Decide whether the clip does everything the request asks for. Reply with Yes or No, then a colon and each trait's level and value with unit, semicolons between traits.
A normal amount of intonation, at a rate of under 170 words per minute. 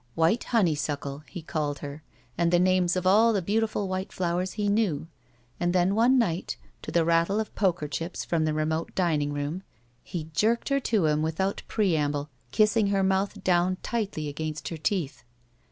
No: average, 4.3 semitones; average, 180 wpm